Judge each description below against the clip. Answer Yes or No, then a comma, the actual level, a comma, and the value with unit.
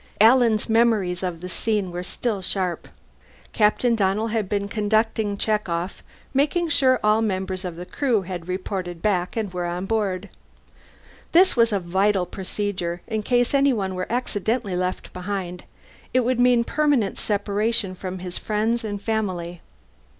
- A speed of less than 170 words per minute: Yes, average, 150 wpm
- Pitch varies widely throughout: No, average, 3.6 semitones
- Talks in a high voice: Yes, high, 205 Hz